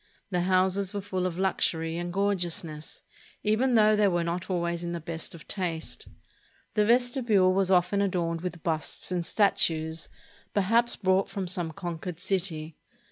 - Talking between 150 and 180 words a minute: Yes, average, 155 wpm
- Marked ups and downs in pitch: No, average, 2.8 semitones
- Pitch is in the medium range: Yes, medium, 180 Hz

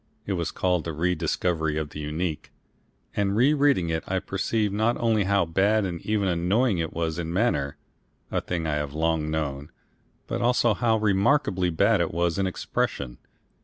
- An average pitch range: Yes, average, 4.4 semitones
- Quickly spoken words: No, average, 175 wpm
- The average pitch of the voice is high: No, very low, 90 Hz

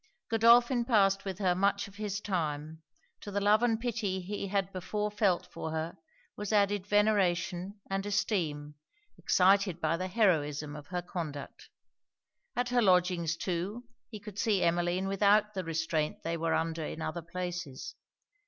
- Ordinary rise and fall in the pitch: Yes, average, 3.6 semitones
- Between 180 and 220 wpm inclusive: No, average, 155 wpm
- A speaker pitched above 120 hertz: Yes, high, 190 Hz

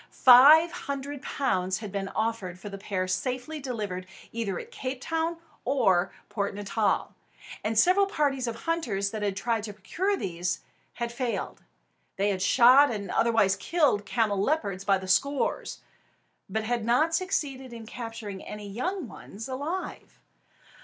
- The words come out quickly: No, average, 145 wpm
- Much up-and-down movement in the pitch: Yes, wide, 5.8 semitones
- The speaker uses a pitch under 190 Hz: No, high, 230 Hz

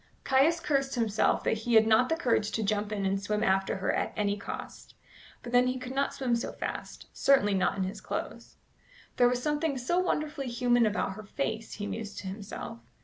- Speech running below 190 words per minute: No, fast, 205 wpm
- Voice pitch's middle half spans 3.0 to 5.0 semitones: Yes, average, 4.4 semitones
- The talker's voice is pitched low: No, high, 230 Hz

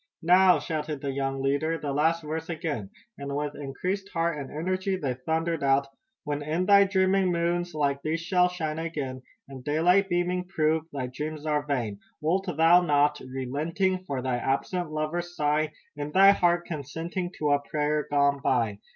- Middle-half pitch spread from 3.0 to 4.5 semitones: Yes, average, 3.6 semitones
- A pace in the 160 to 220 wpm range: Yes, average, 170 wpm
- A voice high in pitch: No, medium, 155 Hz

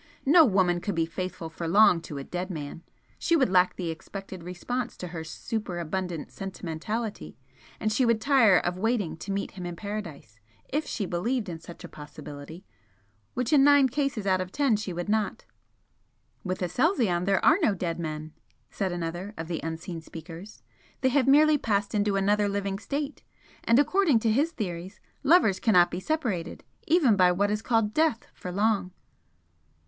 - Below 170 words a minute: No, average, 175 wpm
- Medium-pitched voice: No, high, 195 Hz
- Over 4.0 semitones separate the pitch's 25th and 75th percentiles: Yes, average, 5.0 semitones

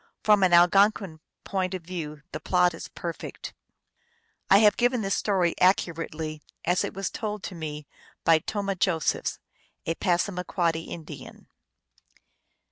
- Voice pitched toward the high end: No, medium, 180 Hz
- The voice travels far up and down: No, average, 3.1 semitones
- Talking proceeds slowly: Yes, slow, 130 wpm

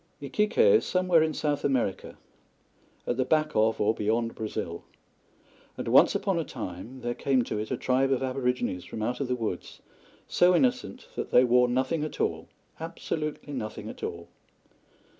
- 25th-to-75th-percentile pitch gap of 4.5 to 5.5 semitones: Yes, average, 5.0 semitones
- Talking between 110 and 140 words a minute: No, average, 170 wpm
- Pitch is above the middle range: No, low, 130 Hz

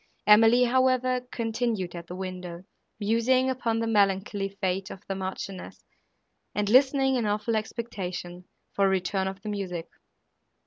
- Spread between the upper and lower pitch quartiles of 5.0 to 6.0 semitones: No, average, 3.7 semitones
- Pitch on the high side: Yes, high, 205 Hz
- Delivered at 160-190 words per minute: No, average, 140 wpm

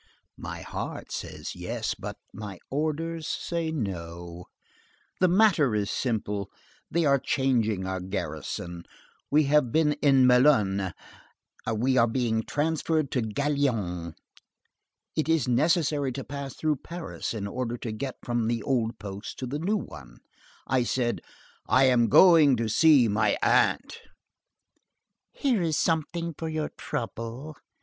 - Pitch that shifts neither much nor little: No, wide, 6.0 semitones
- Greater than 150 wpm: No, slow, 135 wpm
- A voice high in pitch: No, low, 130 Hz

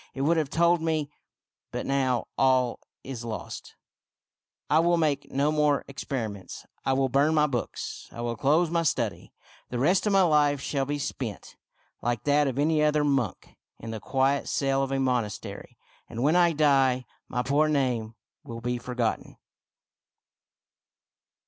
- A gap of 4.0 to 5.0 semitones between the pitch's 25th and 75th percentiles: No, average, 3.5 semitones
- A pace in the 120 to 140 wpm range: No, average, 160 wpm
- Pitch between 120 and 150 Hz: Yes, low, 135 Hz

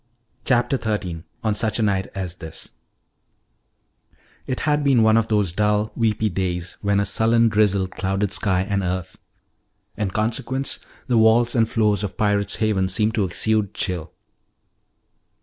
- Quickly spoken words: No, average, 150 wpm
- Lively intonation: No, average, 2.8 semitones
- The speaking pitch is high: No, low, 105 Hz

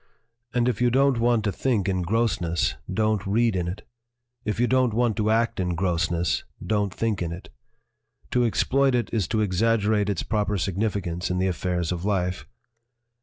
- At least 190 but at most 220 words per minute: Yes, average, 195 wpm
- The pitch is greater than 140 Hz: No, low, 105 Hz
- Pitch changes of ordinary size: Yes, average, 4.2 semitones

